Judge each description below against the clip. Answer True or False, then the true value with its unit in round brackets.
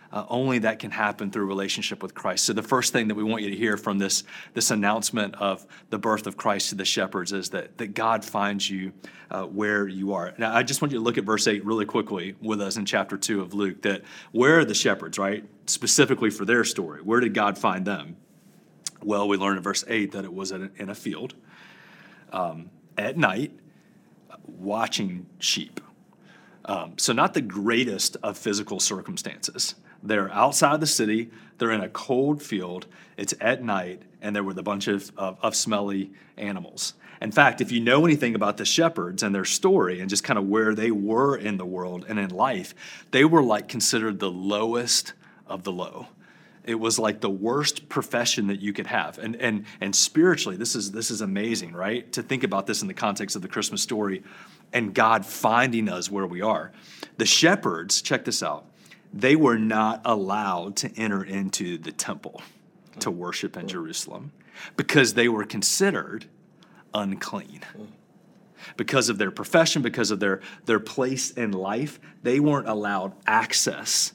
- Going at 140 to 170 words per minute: False (190 wpm)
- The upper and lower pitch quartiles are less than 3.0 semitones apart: True (2.6 semitones)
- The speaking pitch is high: False (105 Hz)